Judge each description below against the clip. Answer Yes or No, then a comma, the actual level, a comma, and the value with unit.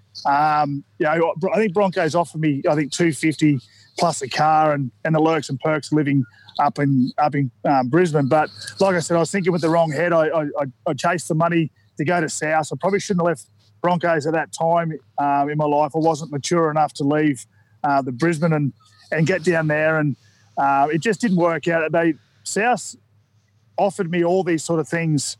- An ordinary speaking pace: No, fast, 215 wpm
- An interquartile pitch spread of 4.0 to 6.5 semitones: No, average, 3.3 semitones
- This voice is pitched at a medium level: Yes, medium, 155 Hz